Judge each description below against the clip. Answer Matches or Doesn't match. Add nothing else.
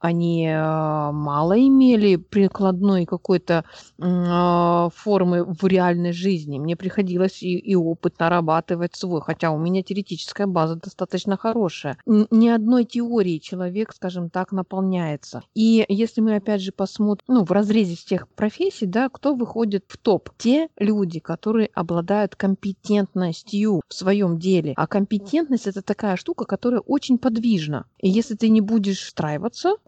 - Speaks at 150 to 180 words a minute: Doesn't match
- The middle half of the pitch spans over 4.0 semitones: Doesn't match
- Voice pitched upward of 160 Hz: Matches